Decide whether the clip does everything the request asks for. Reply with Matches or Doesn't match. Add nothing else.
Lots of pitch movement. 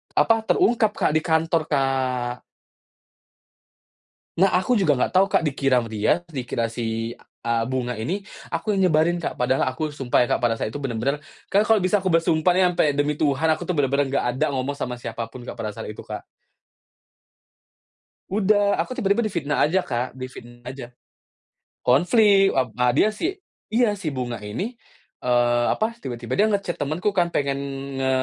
Matches